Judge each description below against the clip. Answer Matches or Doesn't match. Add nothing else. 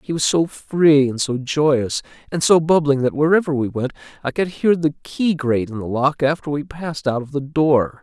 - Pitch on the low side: Doesn't match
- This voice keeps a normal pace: Doesn't match